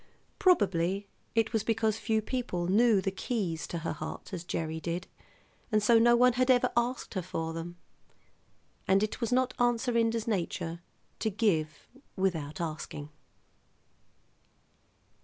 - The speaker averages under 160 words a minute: Yes, average, 140 wpm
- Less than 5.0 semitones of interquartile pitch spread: No, wide, 5.4 semitones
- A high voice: Yes, high, 205 Hz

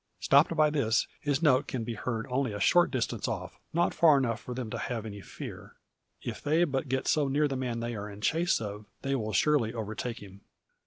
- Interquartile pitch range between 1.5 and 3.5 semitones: No, average, 4.6 semitones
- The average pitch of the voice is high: No, low, 125 Hz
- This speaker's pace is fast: Yes, fast, 220 wpm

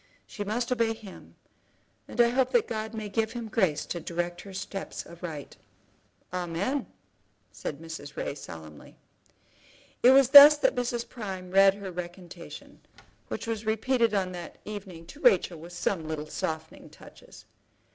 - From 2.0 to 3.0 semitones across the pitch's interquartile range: No, average, 5.2 semitones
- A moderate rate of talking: Yes, average, 150 wpm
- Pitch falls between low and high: No, high, 195 Hz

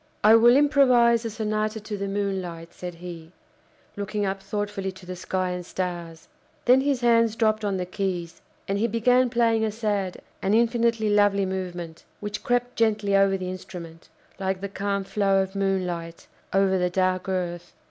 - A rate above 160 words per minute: Yes, average, 170 wpm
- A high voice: Yes, high, 195 Hz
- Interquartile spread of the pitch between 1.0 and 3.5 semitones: Yes, average, 3.1 semitones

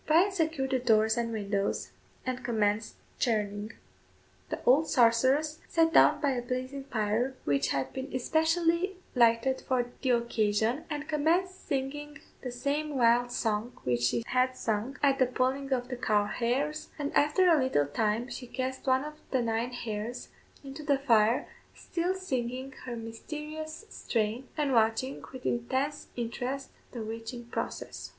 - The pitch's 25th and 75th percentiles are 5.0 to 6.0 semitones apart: No, average, 3.9 semitones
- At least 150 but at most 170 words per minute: Yes, average, 155 wpm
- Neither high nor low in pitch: No, very high, 255 Hz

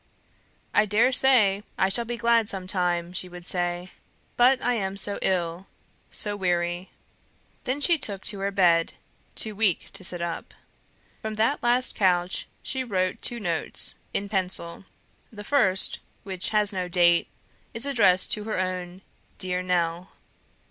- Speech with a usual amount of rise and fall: Yes, average, 3.5 semitones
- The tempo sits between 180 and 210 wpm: No, average, 155 wpm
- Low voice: No, high, 190 Hz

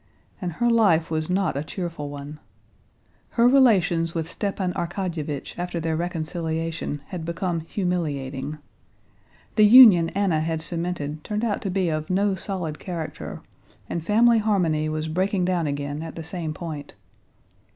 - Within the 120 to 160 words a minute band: Yes, average, 145 wpm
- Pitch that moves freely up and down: No, average, 3.3 semitones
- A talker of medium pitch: Yes, medium, 170 Hz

